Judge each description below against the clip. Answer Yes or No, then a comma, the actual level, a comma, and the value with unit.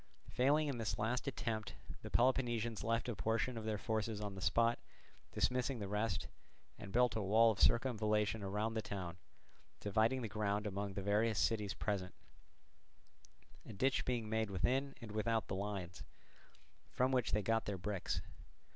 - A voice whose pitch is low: Yes, low, 110 Hz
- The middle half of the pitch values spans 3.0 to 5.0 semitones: No, narrow, 2.4 semitones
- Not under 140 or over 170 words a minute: Yes, average, 165 wpm